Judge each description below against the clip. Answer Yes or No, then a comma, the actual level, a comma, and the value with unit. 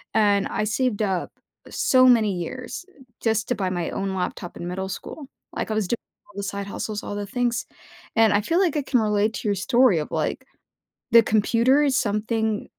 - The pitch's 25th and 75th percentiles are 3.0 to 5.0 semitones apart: Yes, average, 3.4 semitones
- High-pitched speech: Yes, high, 215 Hz